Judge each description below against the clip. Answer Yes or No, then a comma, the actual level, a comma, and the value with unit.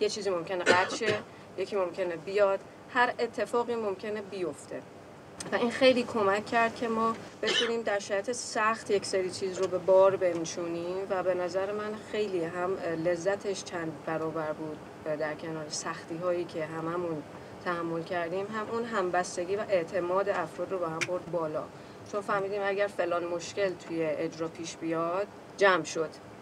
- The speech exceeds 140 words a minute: Yes, fast, 155 wpm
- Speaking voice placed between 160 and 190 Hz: Yes, medium, 185 Hz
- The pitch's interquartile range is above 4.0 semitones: No, average, 3.3 semitones